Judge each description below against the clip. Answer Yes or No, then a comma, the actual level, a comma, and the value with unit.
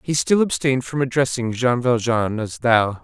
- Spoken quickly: No, average, 180 wpm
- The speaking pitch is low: Yes, low, 120 Hz